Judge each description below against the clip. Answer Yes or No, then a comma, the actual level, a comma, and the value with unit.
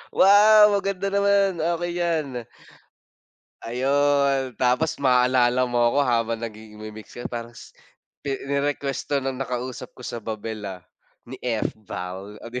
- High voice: No, low, 130 Hz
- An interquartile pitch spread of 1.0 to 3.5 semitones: No, average, 4.8 semitones